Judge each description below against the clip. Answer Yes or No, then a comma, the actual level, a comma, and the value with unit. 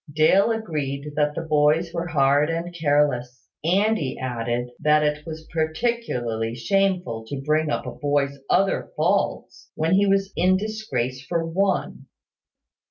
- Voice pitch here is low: No, medium, 155 Hz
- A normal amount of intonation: Yes, average, 4.5 semitones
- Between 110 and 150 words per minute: Yes, average, 145 wpm